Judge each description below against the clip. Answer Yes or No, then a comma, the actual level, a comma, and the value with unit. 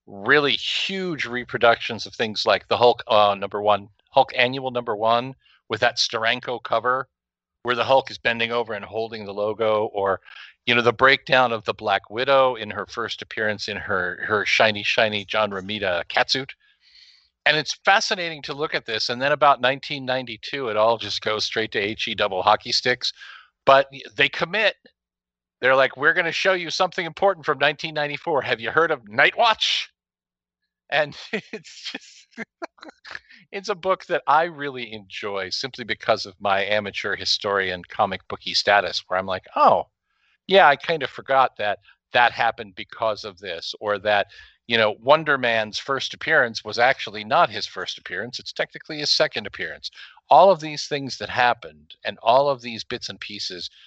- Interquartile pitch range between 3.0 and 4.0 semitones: No, wide, 5.5 semitones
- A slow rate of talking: No, average, 175 wpm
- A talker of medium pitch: No, low, 120 Hz